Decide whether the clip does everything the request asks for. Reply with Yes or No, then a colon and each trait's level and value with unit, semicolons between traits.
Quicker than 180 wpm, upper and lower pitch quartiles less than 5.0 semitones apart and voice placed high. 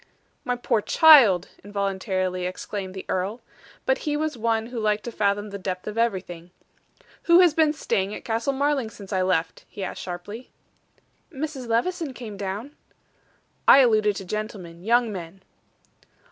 No: average, 155 wpm; average, 4.6 semitones; high, 215 Hz